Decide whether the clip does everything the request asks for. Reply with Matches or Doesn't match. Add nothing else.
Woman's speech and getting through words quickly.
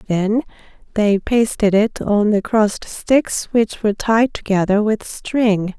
Doesn't match